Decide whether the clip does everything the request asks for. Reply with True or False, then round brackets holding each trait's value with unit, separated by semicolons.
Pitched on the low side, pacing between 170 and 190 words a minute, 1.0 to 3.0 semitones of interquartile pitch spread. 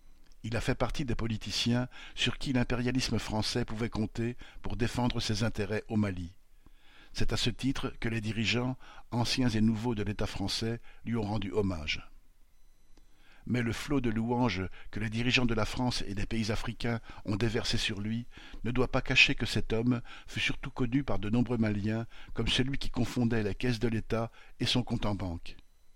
True (115 Hz; 185 wpm; 2.5 semitones)